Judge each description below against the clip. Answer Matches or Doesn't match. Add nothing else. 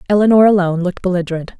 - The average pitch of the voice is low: Doesn't match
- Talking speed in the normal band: Matches